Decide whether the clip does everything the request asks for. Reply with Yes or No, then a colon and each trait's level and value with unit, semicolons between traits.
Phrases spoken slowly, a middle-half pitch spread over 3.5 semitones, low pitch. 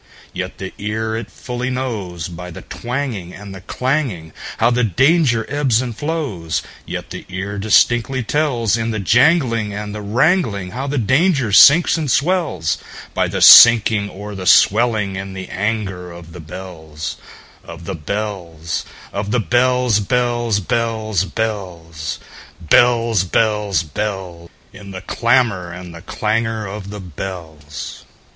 Yes: slow, 120 wpm; average, 4.6 semitones; low, 105 Hz